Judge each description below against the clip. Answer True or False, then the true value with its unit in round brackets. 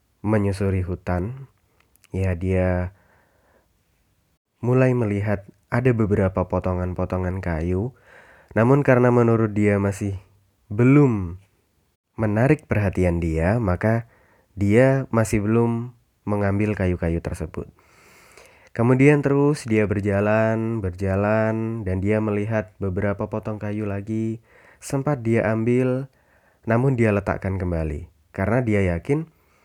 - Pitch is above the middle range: False (105 Hz)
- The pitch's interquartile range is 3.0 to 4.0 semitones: True (3.6 semitones)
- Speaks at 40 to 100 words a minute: True (95 wpm)